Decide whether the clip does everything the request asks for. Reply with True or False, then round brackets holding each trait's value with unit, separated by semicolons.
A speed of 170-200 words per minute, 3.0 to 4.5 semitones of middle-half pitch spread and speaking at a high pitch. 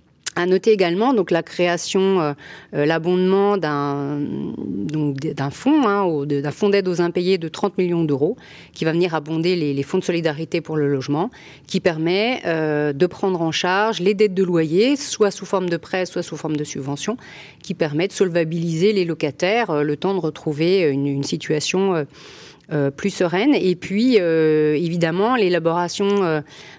False (175 wpm; 3.9 semitones; 170 Hz)